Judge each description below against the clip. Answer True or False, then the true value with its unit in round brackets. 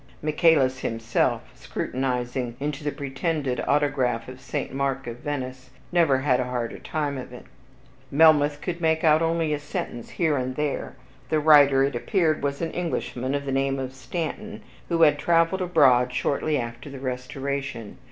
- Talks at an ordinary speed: True (160 wpm)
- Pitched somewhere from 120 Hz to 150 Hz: True (140 Hz)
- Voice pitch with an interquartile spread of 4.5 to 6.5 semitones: False (3.3 semitones)